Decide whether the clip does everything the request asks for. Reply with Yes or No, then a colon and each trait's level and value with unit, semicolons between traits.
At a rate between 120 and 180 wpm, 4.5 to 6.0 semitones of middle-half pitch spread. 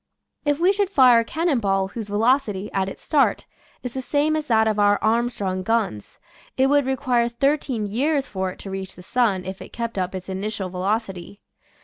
No: average, 200 wpm; wide, 5.5 semitones